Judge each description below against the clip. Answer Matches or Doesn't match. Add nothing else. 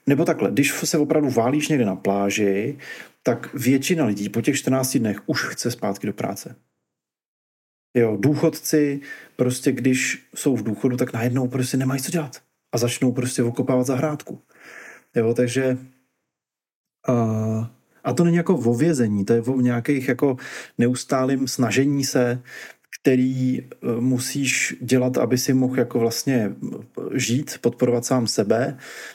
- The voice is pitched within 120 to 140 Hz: Matches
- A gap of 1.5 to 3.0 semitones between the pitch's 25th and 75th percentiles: Matches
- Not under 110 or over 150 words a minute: Matches